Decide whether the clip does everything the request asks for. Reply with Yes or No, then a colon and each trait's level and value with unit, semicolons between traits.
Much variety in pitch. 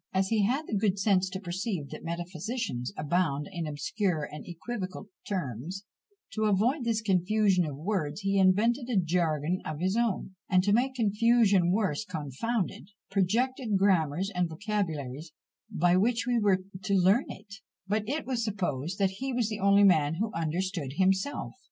No: average, 4.1 semitones